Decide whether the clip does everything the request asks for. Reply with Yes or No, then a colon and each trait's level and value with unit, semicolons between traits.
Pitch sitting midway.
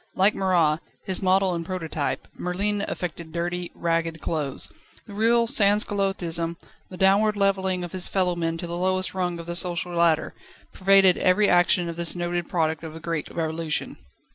Yes: medium, 175 Hz